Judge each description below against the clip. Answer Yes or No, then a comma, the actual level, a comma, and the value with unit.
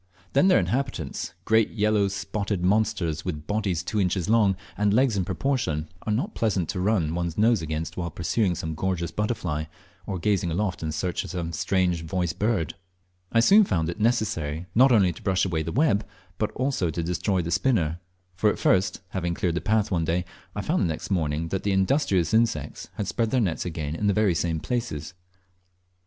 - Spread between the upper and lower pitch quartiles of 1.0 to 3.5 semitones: No, average, 4.4 semitones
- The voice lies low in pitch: Yes, very low, 95 Hz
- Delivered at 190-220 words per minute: Yes, average, 200 wpm